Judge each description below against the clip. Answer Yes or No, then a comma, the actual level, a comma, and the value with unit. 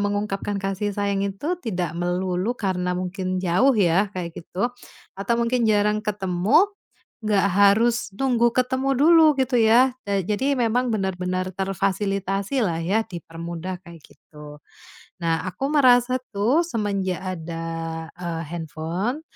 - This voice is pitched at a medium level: No, high, 200 Hz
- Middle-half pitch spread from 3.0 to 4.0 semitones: No, average, 4.8 semitones